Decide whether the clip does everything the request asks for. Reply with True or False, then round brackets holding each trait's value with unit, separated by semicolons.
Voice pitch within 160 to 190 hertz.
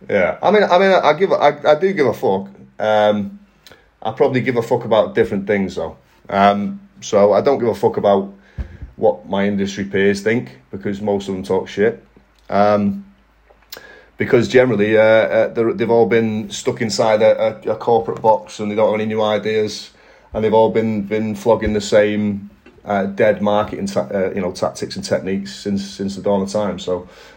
False (105 Hz)